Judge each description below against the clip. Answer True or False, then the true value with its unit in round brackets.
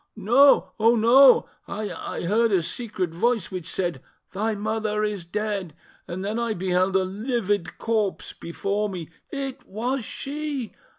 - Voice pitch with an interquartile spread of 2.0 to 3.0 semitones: False (3.8 semitones)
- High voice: True (210 Hz)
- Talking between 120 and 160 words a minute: True (140 wpm)